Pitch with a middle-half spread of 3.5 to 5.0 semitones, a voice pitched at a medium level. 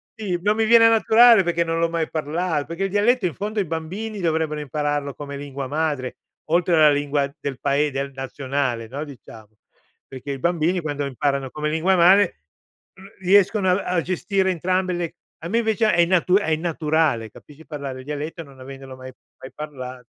Yes: average, 4.6 semitones; medium, 160 Hz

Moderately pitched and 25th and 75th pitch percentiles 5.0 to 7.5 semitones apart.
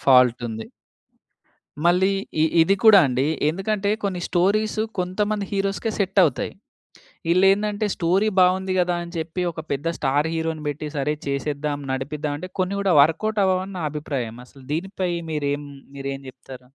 Yes: medium, 170 Hz; average, 5.3 semitones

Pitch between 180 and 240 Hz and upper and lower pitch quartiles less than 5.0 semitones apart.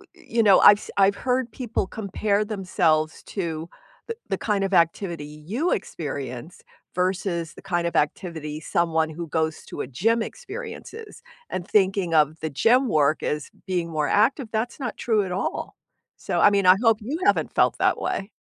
No: high, 190 Hz; average, 5.3 semitones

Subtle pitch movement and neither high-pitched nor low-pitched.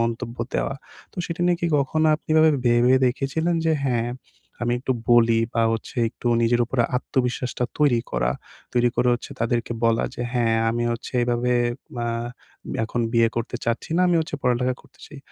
No: narrow, 2.3 semitones; low, 120 Hz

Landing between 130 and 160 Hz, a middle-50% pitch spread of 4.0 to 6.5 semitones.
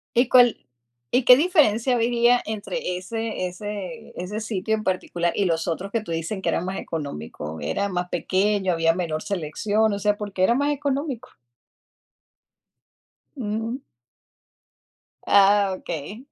No: high, 205 Hz; average, 4.3 semitones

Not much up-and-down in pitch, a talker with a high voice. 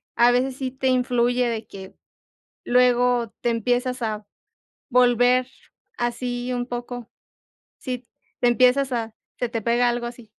Yes: narrow, 0.9 semitones; high, 245 Hz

